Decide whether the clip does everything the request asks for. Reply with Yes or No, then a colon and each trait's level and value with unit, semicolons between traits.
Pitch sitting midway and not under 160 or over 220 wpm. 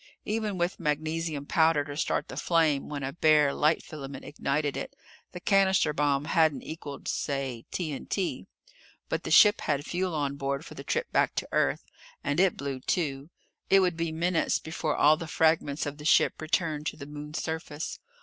Yes: medium, 155 Hz; average, 180 wpm